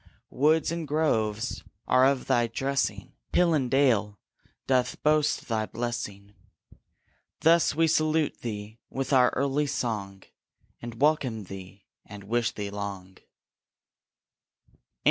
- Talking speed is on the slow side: Yes, slow, 115 wpm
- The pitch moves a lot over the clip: Yes, wide, 5.9 semitones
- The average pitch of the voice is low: Yes, low, 120 Hz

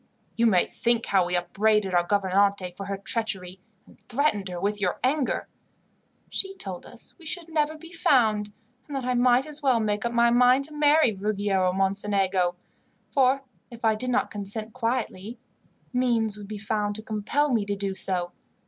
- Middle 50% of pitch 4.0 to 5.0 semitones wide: Yes, average, 4.3 semitones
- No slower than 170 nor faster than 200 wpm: Yes, average, 180 wpm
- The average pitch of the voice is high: Yes, high, 215 Hz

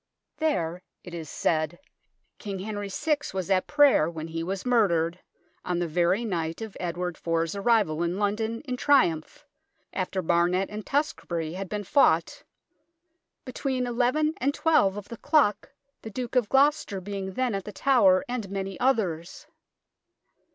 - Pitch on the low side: No, high, 200 Hz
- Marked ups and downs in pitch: Yes, wide, 6.2 semitones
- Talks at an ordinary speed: Yes, average, 155 wpm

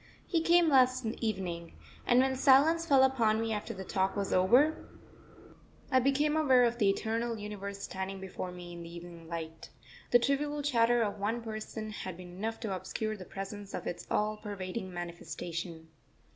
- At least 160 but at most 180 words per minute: Yes, average, 170 wpm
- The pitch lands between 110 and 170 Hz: No, high, 215 Hz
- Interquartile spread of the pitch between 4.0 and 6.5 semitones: Yes, average, 5.2 semitones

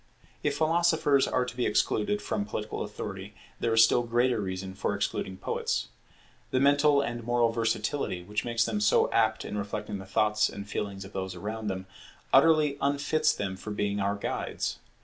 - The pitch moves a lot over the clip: No, average, 4.1 semitones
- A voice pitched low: Yes, low, 110 Hz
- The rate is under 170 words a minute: No, average, 175 wpm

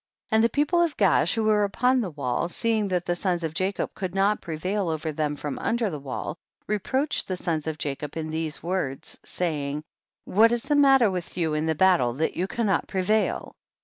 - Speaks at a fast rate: Yes, fast, 215 wpm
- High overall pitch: No, medium, 180 Hz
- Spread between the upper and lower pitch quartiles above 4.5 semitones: Yes, wide, 5.5 semitones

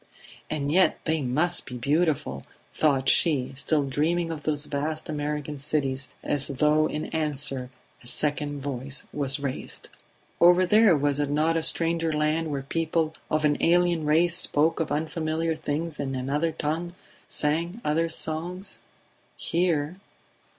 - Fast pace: No, average, 145 wpm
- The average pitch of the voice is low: No, medium, 155 Hz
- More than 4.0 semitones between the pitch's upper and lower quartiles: No, narrow, 2.4 semitones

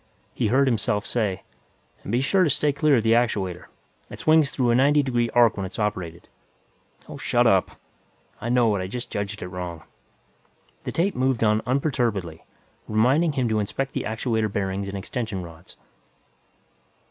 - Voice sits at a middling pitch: No, low, 115 Hz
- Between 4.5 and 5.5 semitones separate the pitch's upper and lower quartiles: Yes, average, 4.8 semitones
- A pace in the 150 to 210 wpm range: Yes, average, 170 wpm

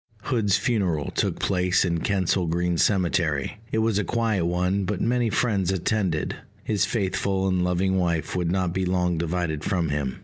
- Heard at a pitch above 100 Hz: No, very low, 90 Hz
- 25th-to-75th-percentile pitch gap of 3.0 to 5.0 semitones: No, narrow, 2.6 semitones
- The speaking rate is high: No, average, 170 wpm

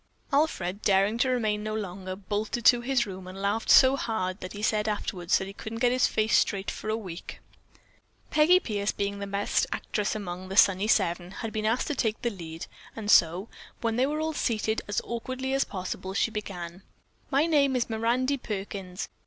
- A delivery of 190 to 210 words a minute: Yes, average, 195 wpm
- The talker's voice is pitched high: Yes, high, 210 Hz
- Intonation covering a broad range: No, average, 3.8 semitones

